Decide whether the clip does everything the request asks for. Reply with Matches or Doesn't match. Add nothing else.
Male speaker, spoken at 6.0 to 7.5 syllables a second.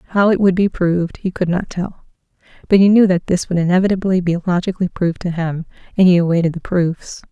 Doesn't match